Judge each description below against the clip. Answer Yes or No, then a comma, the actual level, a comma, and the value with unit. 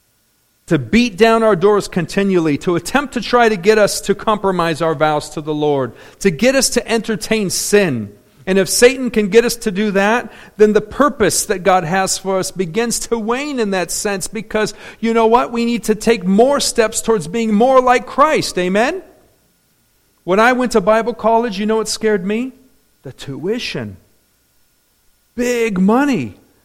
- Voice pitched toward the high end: Yes, high, 215 Hz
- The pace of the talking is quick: No, average, 180 wpm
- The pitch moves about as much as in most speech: Yes, average, 3.5 semitones